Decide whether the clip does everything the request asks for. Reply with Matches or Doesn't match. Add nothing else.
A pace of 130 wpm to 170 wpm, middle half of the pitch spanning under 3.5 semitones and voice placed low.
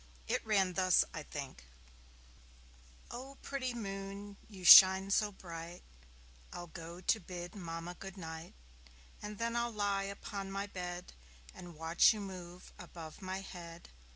Doesn't match